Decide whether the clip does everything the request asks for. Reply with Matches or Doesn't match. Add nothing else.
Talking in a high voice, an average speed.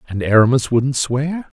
Doesn't match